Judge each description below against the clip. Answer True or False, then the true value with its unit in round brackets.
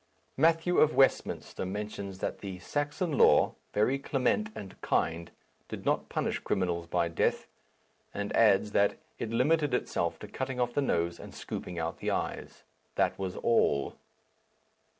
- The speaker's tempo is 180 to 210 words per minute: False (150 wpm)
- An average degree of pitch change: False (7.1 semitones)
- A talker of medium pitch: False (105 Hz)